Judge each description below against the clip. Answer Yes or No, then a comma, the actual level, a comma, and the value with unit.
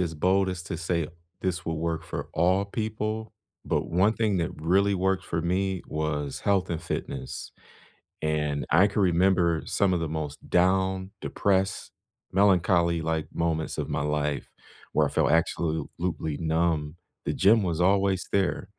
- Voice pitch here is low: Yes, very low, 85 Hz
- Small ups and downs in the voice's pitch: No, average, 3.1 semitones